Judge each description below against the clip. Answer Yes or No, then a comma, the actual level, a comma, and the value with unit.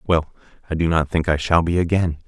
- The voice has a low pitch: Yes, very low, 85 Hz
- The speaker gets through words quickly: Yes, fast, 240 wpm